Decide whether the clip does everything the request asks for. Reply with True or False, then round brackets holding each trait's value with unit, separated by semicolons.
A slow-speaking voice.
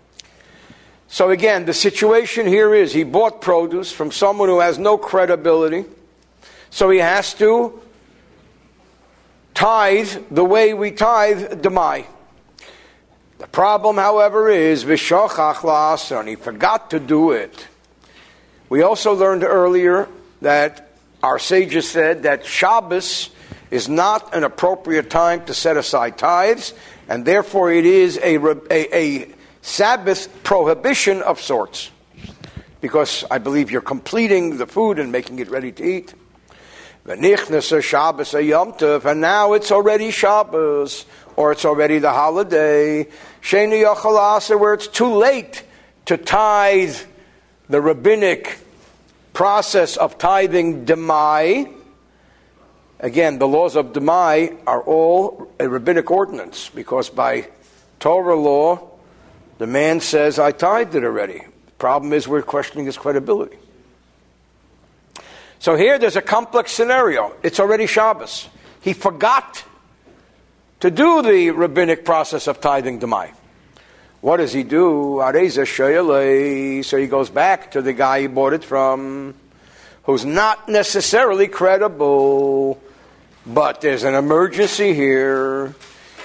True (120 wpm)